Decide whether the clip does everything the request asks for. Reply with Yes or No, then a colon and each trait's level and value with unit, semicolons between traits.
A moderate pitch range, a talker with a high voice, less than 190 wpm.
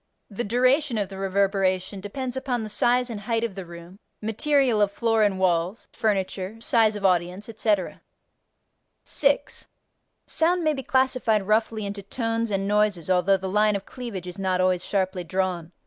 Yes: average, 3.5 semitones; high, 205 Hz; average, 165 wpm